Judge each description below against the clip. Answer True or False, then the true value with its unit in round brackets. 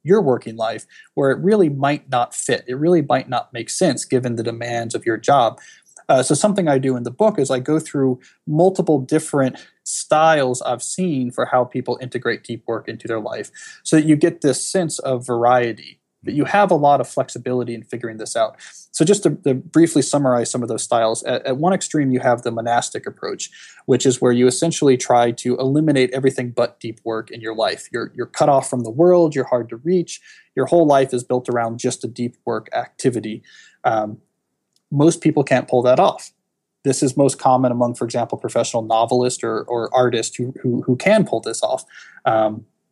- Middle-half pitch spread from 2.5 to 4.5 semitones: True (3.7 semitones)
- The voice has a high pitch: False (130 Hz)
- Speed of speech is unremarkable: False (210 wpm)